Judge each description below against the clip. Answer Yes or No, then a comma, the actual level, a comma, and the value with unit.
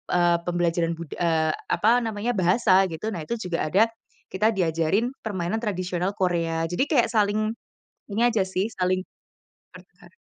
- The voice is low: No, medium, 185 Hz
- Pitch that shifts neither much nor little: Yes, average, 4.0 semitones